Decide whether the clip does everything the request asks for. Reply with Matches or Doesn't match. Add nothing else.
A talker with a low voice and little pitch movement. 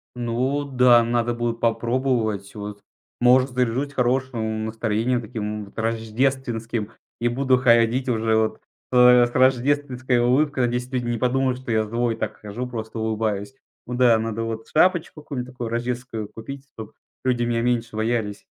Matches